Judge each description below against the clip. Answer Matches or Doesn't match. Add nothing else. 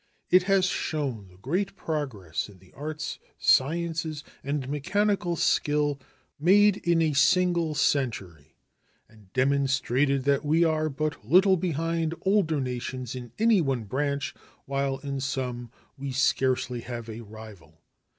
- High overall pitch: Doesn't match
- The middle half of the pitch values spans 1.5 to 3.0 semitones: Doesn't match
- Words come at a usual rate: Doesn't match